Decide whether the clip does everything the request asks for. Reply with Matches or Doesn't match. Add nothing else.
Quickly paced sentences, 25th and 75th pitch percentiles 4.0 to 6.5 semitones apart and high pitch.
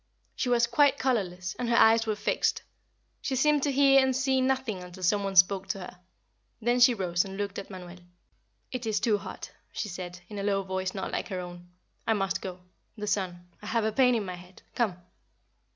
Matches